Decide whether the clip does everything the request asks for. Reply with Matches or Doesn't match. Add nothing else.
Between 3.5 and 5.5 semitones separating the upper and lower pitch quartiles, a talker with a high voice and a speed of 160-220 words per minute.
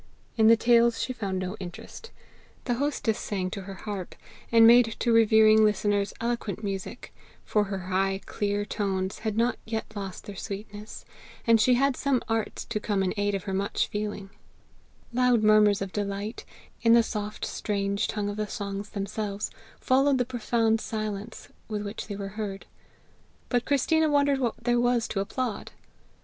Doesn't match